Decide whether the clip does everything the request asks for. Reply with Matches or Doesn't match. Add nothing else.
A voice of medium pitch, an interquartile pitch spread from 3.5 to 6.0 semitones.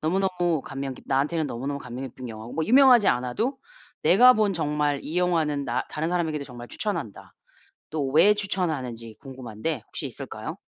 Matches